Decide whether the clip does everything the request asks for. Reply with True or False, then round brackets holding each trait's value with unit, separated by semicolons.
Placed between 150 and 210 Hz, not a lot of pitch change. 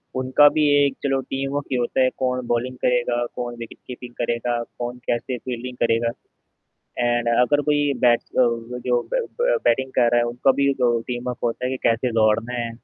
False (125 Hz; 1.5 semitones)